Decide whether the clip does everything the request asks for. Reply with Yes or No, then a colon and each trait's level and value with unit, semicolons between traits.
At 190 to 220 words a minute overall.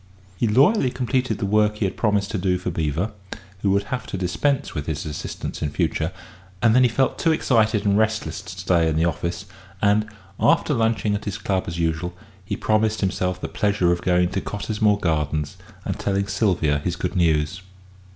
Yes: average, 195 wpm